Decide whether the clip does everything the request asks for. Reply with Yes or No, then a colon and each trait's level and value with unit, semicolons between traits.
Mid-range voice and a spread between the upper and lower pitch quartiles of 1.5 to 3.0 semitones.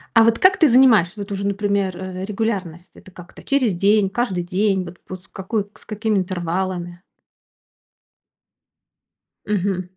No: high, 195 Hz; average, 2.7 semitones